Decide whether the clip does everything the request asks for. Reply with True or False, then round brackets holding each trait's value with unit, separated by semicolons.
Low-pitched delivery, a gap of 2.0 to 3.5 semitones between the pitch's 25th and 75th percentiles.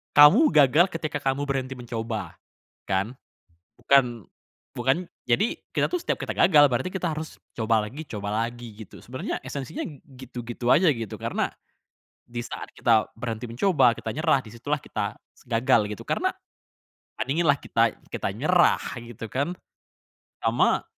False (125 Hz; 4.2 semitones)